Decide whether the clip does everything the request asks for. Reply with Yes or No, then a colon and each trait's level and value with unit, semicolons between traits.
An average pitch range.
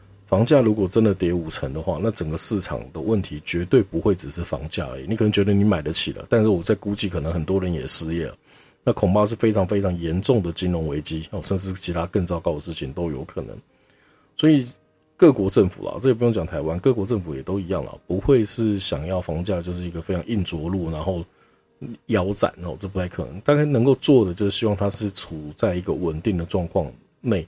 Yes: average, 4.3 semitones